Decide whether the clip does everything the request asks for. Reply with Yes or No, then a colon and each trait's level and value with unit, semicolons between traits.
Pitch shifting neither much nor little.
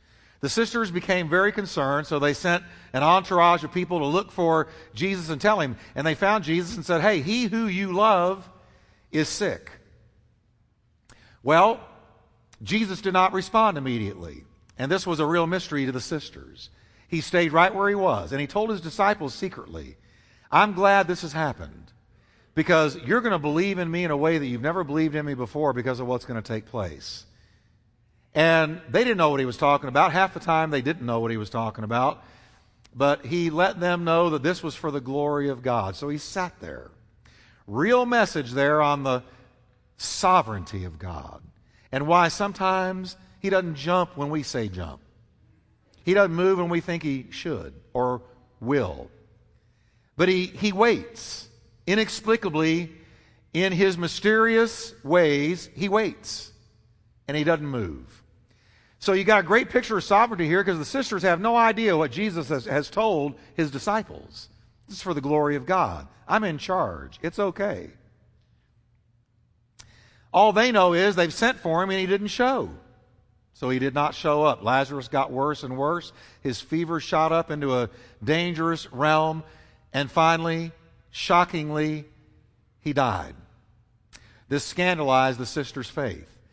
No: wide, 7.6 semitones